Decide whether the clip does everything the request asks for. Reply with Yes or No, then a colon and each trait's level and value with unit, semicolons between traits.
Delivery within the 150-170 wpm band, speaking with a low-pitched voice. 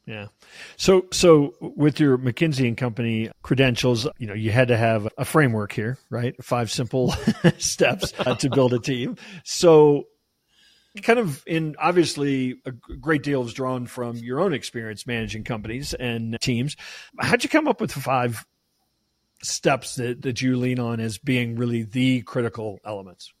Yes: average, 160 wpm; low, 130 Hz